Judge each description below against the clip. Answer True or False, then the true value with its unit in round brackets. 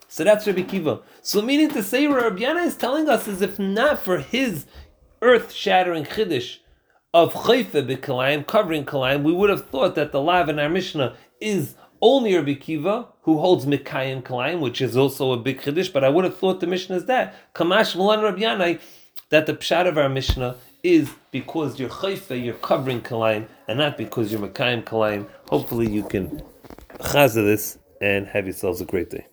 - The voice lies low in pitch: False (160 Hz)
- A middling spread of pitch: False (7.7 semitones)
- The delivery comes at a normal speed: True (190 wpm)